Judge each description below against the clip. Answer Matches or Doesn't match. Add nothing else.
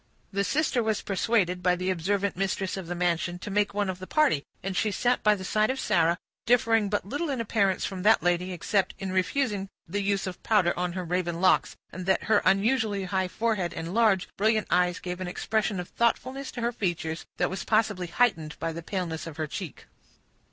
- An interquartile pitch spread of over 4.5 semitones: Doesn't match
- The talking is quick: Matches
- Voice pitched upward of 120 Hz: Matches